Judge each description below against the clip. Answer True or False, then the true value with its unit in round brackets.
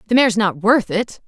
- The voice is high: True (215 Hz)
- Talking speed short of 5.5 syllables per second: False (5.9 syllables/s)